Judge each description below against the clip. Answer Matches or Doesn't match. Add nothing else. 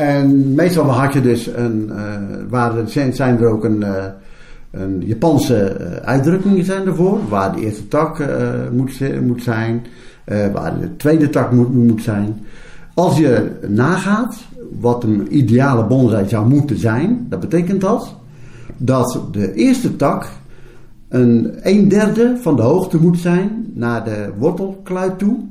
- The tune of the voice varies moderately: Doesn't match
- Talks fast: Doesn't match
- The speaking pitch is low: Matches